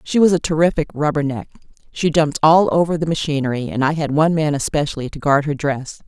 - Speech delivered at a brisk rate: Yes, fast, 210 wpm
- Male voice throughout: No, female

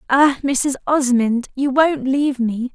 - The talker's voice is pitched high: Yes, very high, 265 Hz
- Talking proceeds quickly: No, average, 155 wpm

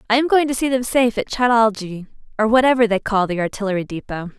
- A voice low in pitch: No, high, 225 Hz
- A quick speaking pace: Yes, fast, 220 wpm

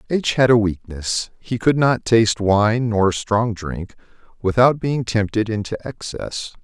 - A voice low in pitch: Yes, low, 110 Hz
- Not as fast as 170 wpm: Yes, average, 155 wpm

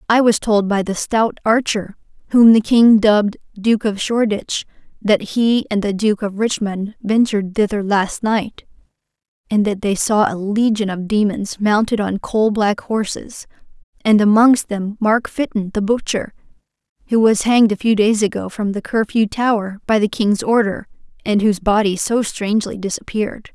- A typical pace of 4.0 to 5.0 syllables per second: Yes, 4.7 syllables/s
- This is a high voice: Yes, high, 210 Hz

